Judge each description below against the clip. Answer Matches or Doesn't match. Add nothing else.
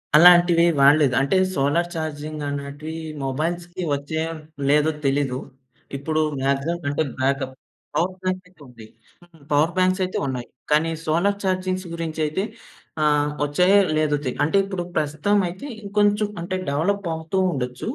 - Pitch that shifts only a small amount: Doesn't match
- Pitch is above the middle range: Doesn't match